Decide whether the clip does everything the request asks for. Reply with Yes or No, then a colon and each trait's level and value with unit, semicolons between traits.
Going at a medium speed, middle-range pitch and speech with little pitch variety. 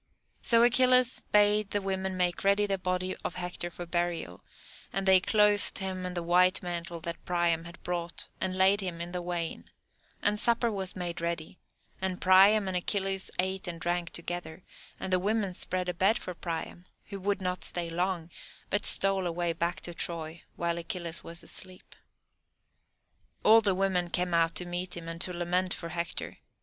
Yes: average, 180 wpm; medium, 180 Hz; narrow, 2.0 semitones